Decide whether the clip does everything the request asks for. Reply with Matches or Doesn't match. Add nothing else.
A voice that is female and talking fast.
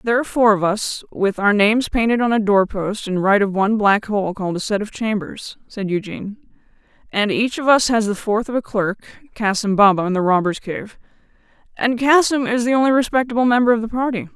Matches